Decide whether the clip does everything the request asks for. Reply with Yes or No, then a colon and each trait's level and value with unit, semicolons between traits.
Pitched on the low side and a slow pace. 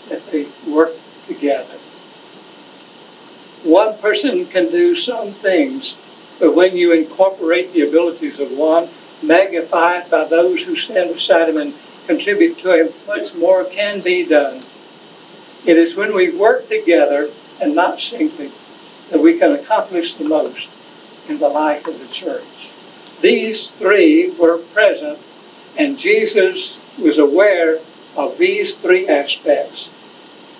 No: medium, 185 Hz; slow, 130 wpm